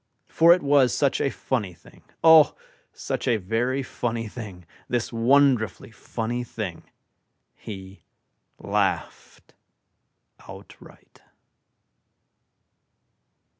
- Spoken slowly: Yes, slow, 90 wpm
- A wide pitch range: No, average, 4.0 semitones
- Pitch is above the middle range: No, low, 120 Hz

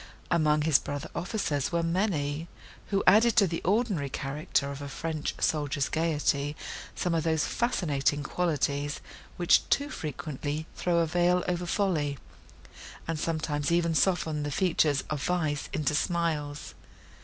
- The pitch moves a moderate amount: Yes, average, 3.2 semitones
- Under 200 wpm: Yes, average, 140 wpm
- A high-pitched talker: No, medium, 160 Hz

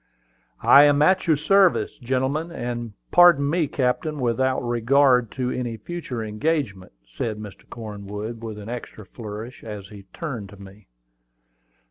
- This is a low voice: Yes, low, 120 Hz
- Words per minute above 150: No, average, 140 wpm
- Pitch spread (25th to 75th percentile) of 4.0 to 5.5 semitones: Yes, average, 5.1 semitones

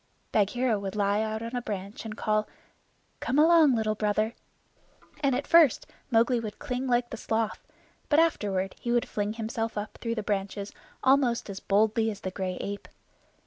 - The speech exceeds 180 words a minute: No, average, 170 wpm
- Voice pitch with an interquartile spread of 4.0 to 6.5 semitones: No, average, 3.0 semitones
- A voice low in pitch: No, high, 220 Hz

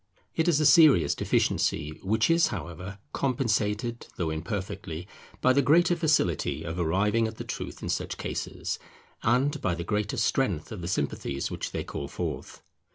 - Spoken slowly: No, average, 160 wpm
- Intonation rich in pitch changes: Yes, wide, 7.7 semitones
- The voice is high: No, low, 105 Hz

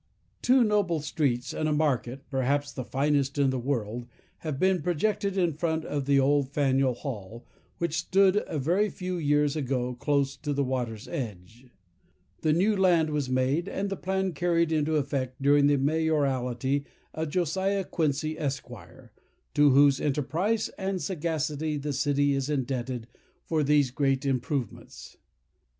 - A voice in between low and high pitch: Yes, medium, 145 Hz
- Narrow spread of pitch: No, average, 3.5 semitones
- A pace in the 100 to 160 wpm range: Yes, average, 150 wpm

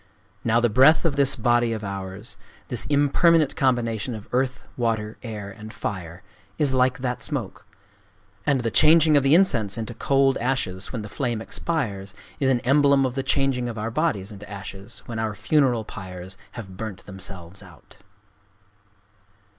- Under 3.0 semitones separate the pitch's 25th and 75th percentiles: No, average, 4.9 semitones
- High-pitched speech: No, low, 115 Hz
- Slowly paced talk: No, average, 155 wpm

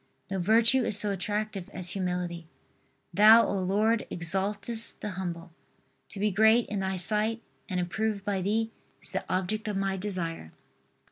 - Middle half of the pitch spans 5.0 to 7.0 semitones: No, average, 2.8 semitones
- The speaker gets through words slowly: No, average, 155 wpm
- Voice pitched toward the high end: Yes, high, 200 Hz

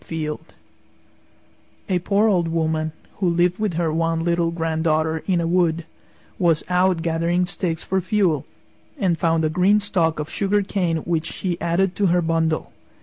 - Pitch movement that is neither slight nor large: No, narrow, 2.0 semitones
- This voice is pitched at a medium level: Yes, medium, 170 Hz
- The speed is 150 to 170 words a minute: Yes, average, 160 wpm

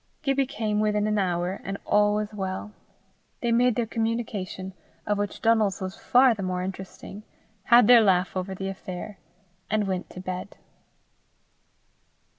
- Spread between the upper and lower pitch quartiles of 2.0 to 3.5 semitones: Yes, average, 2.9 semitones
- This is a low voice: No, high, 205 Hz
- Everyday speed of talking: Yes, average, 150 wpm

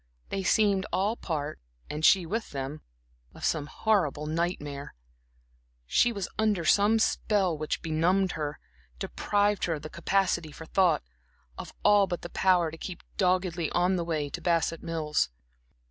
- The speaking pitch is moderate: Yes, medium, 175 Hz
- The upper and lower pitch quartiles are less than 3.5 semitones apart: No, average, 3.9 semitones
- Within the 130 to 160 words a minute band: Yes, average, 155 wpm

